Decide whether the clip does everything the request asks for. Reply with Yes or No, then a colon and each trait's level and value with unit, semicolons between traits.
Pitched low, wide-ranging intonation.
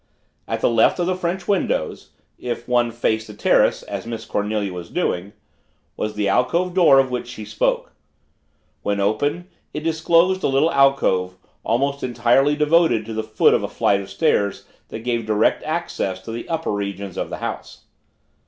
Yes: low, 120 Hz; wide, 6.4 semitones